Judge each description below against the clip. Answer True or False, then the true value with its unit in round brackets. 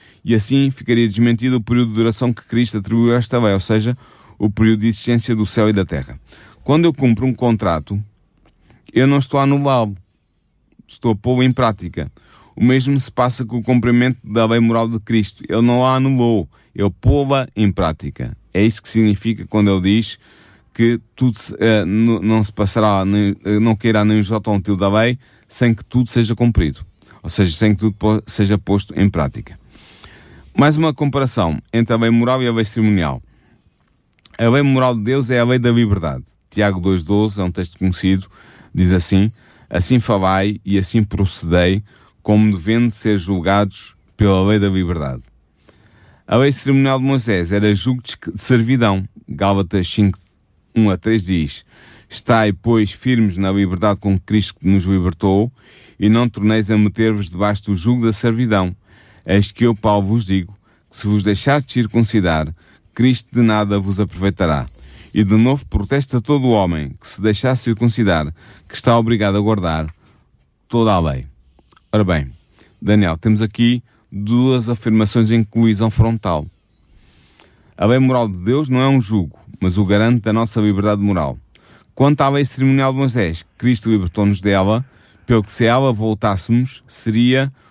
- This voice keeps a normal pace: False (175 wpm)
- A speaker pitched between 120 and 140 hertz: False (110 Hz)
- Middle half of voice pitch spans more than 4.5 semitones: False (3.2 semitones)